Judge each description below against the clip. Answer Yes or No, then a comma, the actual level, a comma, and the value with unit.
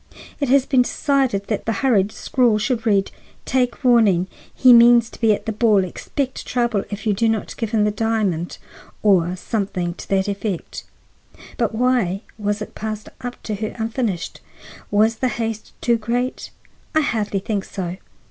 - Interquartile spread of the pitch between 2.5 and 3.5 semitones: Yes, average, 3.1 semitones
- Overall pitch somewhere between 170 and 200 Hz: No, high, 220 Hz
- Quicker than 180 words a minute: No, average, 170 wpm